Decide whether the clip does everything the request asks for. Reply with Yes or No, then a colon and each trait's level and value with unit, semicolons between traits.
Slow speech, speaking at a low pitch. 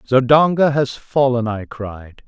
Yes: slow, 130 wpm; low, 125 Hz